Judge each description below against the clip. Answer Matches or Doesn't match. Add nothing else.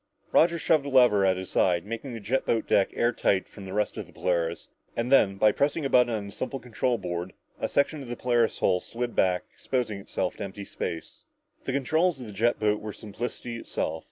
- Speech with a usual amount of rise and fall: Matches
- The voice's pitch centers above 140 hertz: Doesn't match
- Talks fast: Matches